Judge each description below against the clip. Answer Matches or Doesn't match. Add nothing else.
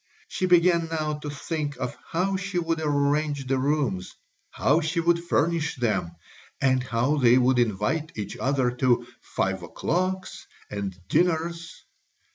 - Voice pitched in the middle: Matches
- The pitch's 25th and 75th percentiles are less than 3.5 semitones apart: Doesn't match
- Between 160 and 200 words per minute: Doesn't match